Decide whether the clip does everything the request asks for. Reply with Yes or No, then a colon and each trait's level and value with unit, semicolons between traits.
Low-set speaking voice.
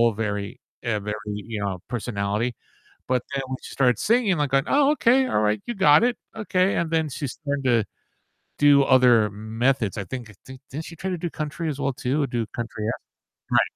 Yes: low, 130 Hz